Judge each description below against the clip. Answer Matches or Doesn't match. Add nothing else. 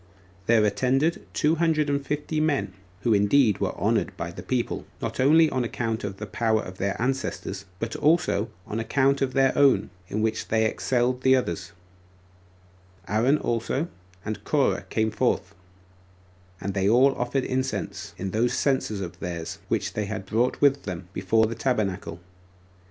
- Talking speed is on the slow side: Doesn't match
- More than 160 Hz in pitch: Doesn't match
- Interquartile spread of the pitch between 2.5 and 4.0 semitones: Doesn't match